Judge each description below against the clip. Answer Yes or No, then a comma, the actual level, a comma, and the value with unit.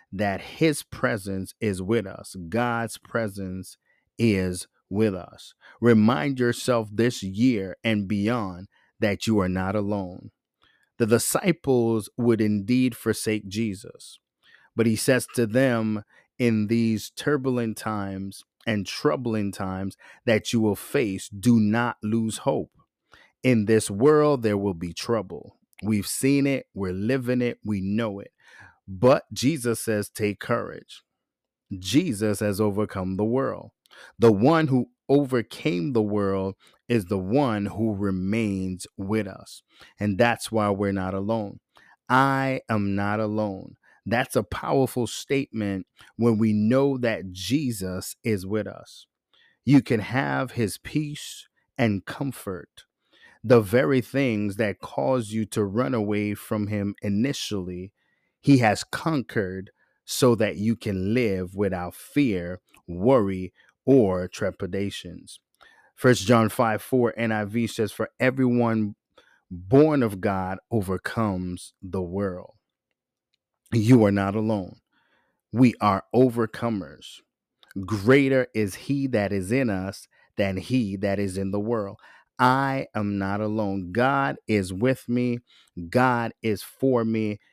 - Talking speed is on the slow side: Yes, slow, 130 wpm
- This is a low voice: Yes, low, 110 Hz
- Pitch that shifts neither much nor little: Yes, average, 3.6 semitones